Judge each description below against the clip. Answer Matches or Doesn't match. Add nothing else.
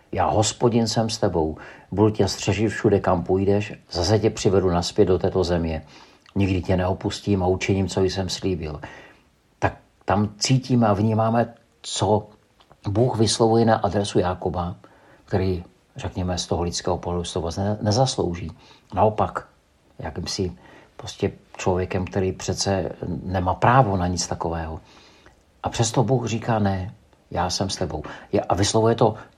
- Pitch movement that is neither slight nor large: Matches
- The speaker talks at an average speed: Matches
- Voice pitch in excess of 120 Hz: Doesn't match